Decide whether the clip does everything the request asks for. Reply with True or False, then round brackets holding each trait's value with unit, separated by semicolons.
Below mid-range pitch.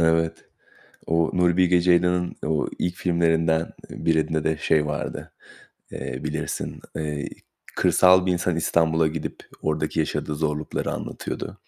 True (80 Hz)